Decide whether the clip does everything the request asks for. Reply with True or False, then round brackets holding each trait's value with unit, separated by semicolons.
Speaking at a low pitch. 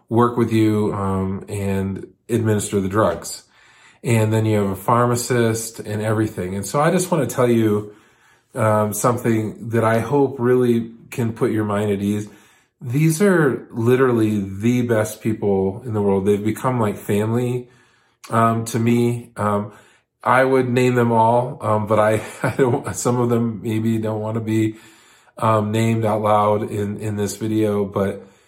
True (110 Hz)